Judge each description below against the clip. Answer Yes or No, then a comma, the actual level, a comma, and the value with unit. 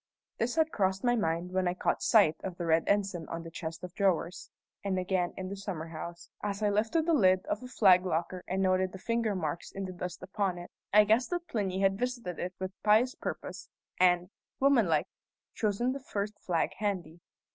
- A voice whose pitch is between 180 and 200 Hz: Yes, high, 190 Hz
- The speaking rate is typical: No, fast, 210 wpm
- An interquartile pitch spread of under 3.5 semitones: Yes, average, 3.0 semitones